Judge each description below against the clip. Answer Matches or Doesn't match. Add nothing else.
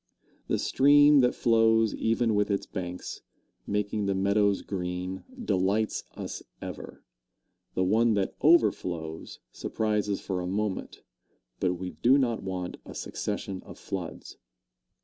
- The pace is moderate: Doesn't match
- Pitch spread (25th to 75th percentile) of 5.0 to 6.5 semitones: Doesn't match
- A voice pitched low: Matches